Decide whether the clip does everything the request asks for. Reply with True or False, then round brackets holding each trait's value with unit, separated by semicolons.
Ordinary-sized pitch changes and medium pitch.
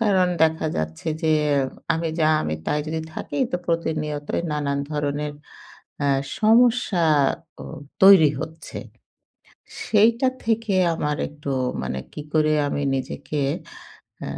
True (4.4 semitones; 155 Hz)